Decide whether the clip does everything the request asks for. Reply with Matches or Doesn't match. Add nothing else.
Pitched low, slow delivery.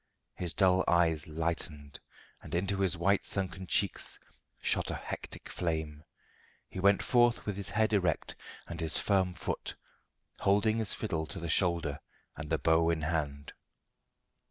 Doesn't match